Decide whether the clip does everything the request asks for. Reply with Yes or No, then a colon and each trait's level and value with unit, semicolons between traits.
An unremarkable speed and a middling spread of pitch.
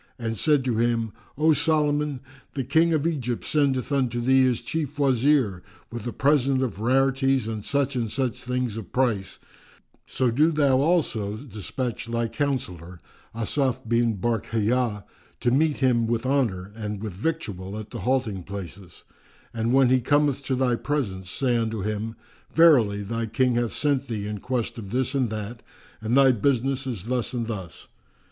Yes: average, 165 wpm; average, 3.7 semitones